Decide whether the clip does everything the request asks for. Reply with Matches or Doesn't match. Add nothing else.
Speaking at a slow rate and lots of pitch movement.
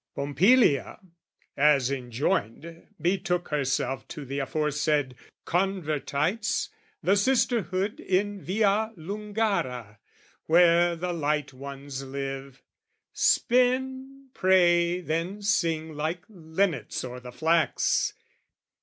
Matches